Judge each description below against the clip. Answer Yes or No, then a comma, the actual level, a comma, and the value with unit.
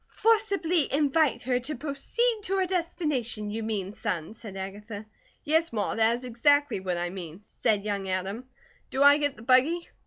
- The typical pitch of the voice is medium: No, very high, 250 Hz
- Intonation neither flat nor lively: No, wide, 6.8 semitones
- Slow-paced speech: No, average, 175 wpm